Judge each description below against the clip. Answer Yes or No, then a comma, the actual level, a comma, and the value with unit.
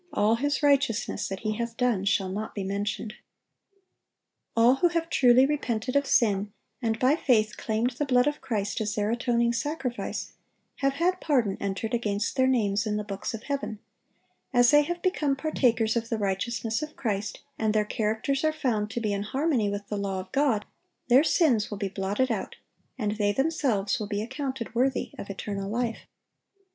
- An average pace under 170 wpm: No, average, 185 wpm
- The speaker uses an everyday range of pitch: Yes, average, 4.4 semitones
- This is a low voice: No, high, 230 Hz